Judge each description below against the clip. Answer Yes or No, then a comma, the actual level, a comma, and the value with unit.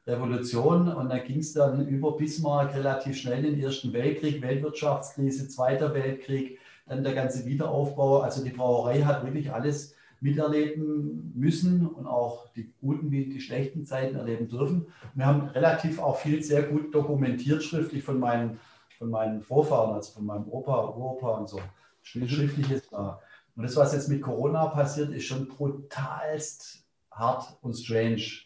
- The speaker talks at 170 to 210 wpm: No, average, 160 wpm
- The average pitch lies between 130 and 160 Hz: Yes, low, 135 Hz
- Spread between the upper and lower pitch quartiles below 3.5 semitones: Yes, average, 3.0 semitones